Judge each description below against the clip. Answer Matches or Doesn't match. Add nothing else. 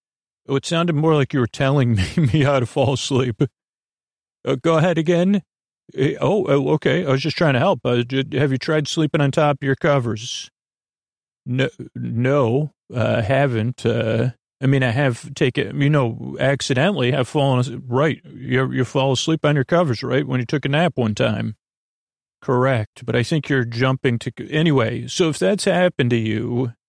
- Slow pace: Doesn't match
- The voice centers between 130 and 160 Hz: Matches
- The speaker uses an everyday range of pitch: Matches